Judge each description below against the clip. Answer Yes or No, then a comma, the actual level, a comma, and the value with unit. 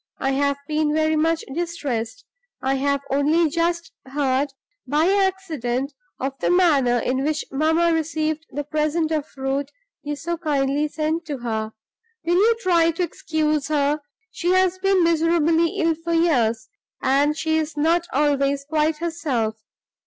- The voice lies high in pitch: Yes, very high, 310 Hz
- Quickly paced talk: No, average, 150 wpm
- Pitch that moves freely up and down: No, average, 3.1 semitones